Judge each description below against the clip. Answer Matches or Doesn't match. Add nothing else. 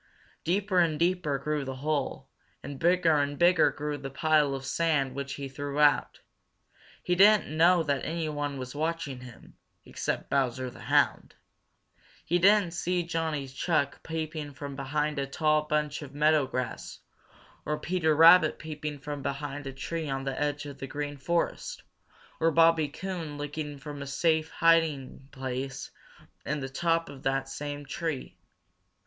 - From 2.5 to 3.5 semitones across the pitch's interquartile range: Matches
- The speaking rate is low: Doesn't match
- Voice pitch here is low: Doesn't match